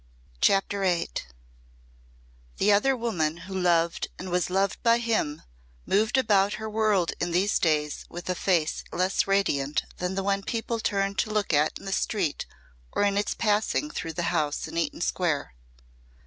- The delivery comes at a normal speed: Yes, average, 165 wpm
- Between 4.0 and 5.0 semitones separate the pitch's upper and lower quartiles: No, average, 3.6 semitones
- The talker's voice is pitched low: No, high, 190 Hz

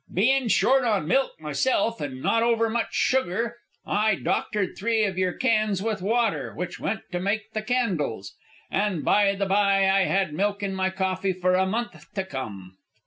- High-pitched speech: Yes, high, 200 Hz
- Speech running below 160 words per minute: No, average, 180 wpm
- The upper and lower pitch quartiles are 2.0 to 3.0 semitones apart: No, average, 3.4 semitones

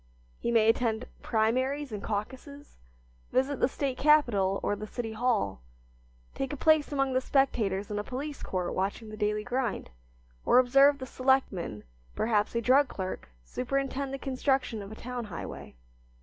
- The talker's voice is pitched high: Yes, high, 245 Hz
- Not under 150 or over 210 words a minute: Yes, average, 160 wpm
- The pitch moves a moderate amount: Yes, average, 4.3 semitones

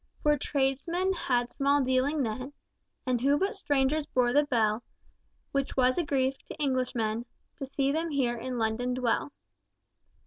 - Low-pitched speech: No, very high, 265 Hz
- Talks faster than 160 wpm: No, average, 150 wpm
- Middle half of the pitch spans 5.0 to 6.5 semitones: No, narrow, 2.6 semitones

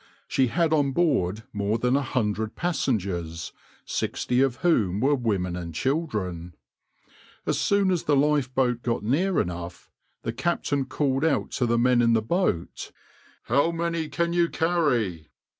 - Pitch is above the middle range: No, low, 125 Hz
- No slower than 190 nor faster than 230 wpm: No, average, 150 wpm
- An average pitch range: No, wide, 7.2 semitones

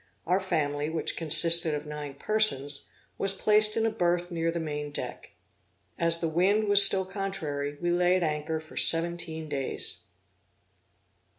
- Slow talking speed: No, average, 155 wpm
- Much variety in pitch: No, average, 3.9 semitones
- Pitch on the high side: No, medium, 165 Hz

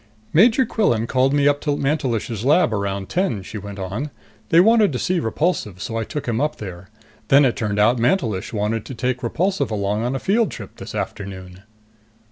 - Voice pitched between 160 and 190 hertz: No, low, 120 Hz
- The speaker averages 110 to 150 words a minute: No, average, 195 wpm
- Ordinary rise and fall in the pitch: No, wide, 6.4 semitones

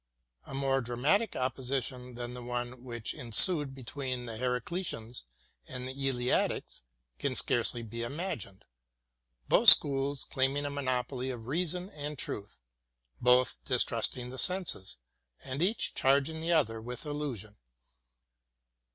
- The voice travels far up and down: No, average, 3.2 semitones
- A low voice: Yes, low, 130 Hz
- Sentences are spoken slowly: Yes, slow, 125 wpm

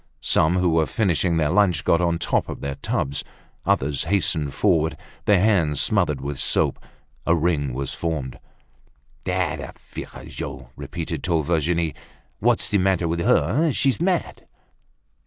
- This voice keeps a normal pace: Yes, average, 150 wpm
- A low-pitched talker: Yes, very low, 85 Hz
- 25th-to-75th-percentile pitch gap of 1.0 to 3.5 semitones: No, average, 3.9 semitones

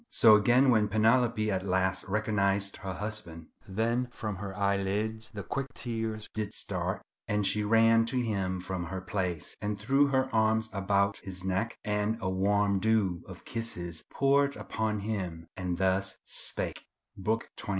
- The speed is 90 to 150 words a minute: No, average, 160 wpm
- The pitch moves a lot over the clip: No, average, 2.7 semitones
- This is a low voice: Yes, low, 105 Hz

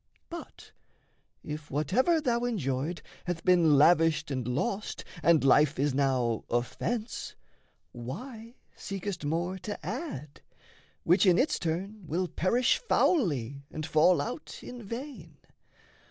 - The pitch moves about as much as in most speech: No, wide, 7.1 semitones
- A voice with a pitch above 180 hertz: No, medium, 175 Hz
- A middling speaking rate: No, slow, 120 wpm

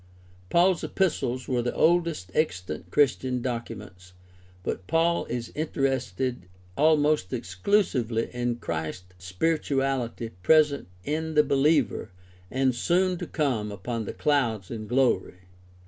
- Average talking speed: No, slow, 115 wpm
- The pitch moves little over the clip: No, wide, 5.6 semitones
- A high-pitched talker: No, low, 130 Hz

